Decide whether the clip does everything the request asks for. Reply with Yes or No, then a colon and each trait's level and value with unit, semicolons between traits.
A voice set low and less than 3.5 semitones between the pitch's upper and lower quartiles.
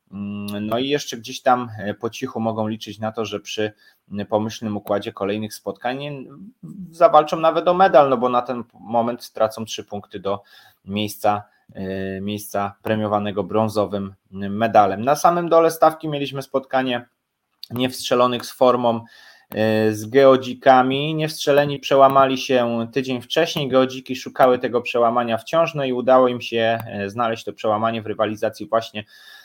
No: low, 120 Hz; average, 3.8 semitones